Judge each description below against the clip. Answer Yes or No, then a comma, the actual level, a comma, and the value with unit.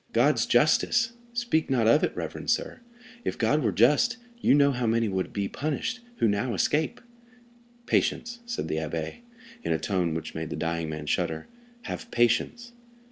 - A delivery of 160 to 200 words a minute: Yes, average, 170 wpm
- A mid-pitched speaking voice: No, low, 115 Hz